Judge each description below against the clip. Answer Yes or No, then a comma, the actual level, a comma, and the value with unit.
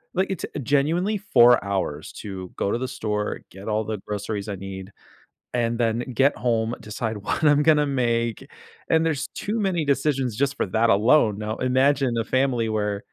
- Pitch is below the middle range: Yes, low, 120 Hz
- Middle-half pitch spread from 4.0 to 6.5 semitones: Yes, average, 5.1 semitones